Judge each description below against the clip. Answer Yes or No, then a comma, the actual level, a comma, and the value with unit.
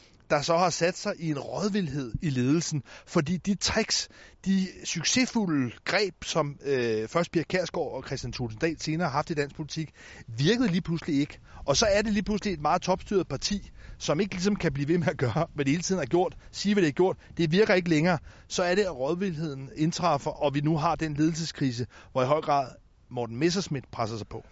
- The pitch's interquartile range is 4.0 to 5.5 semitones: Yes, average, 4.4 semitones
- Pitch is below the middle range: No, medium, 160 Hz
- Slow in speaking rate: No, average, 220 wpm